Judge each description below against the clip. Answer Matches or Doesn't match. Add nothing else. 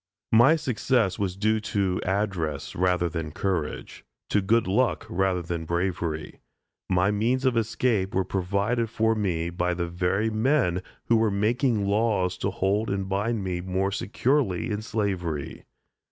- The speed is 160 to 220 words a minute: Doesn't match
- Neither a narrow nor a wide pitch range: Matches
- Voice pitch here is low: Matches